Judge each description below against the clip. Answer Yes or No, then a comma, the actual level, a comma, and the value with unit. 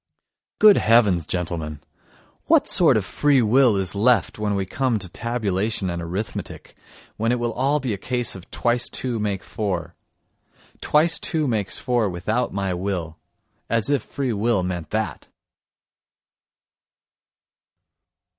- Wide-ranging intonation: No, average, 4.7 semitones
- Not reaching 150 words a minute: Yes, slow, 135 wpm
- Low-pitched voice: Yes, low, 110 Hz